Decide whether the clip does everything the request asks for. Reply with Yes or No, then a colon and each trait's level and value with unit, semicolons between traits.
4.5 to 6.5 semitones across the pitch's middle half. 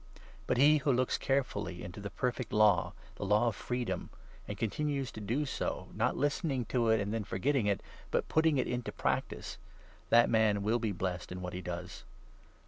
Yes: average, 4.9 semitones